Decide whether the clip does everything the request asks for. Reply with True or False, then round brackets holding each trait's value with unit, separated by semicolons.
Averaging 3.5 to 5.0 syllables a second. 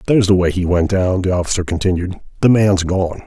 False (6.0 syllables/s)